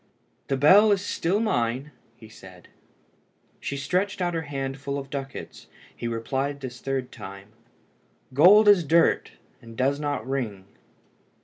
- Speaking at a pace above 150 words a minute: No, average, 140 wpm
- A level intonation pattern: No, average, 5.2 semitones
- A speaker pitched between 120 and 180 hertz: Yes, medium, 140 Hz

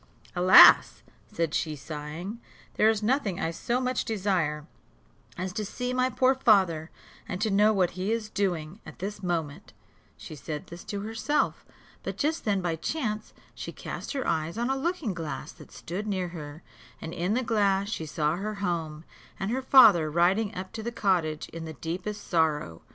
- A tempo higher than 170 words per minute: Yes, average, 180 wpm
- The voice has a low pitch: No, high, 190 Hz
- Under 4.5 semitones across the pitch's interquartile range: No, average, 5.0 semitones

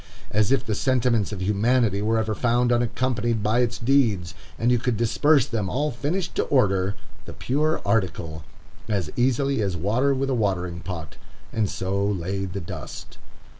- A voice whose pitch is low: Yes, low, 115 Hz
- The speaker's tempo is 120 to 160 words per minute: No, average, 170 wpm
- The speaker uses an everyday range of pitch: Yes, average, 4.4 semitones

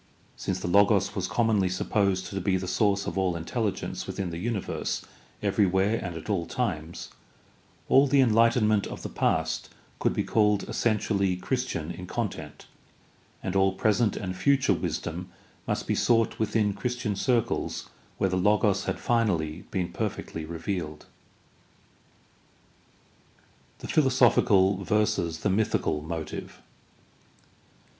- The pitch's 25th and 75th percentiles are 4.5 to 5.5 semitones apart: No, average, 3.6 semitones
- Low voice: Yes, low, 100 Hz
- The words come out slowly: Yes, slow, 130 wpm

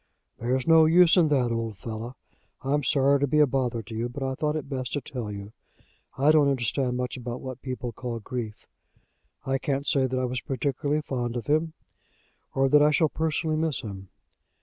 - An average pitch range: Yes, average, 3.5 semitones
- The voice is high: No, low, 130 Hz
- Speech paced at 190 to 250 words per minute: Yes, average, 200 wpm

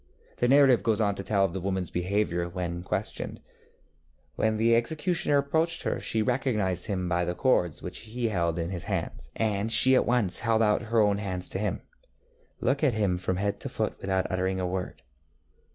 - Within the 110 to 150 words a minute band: No, average, 195 wpm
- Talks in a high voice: No, low, 100 Hz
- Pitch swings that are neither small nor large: Yes, average, 4.2 semitones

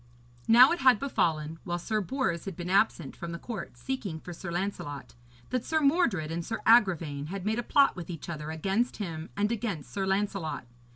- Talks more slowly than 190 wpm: No, average, 195 wpm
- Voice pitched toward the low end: No, high, 190 Hz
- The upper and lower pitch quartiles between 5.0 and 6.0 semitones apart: Yes, wide, 5.5 semitones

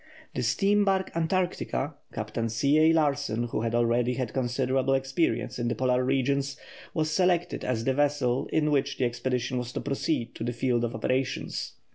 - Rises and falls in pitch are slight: No, average, 3.6 semitones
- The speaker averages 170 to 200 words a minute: Yes, average, 175 wpm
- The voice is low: Yes, low, 130 Hz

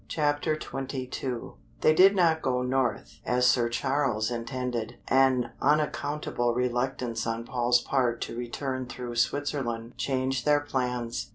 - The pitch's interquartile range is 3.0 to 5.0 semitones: No, narrow, 2.5 semitones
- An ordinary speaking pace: No, slow, 125 wpm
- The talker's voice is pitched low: Yes, low, 125 Hz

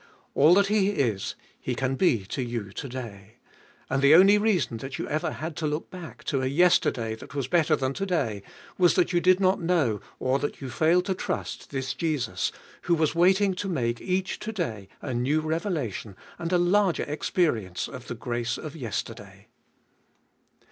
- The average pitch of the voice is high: No, medium, 150 Hz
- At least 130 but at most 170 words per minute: No, average, 190 wpm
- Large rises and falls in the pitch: Yes, wide, 6.5 semitones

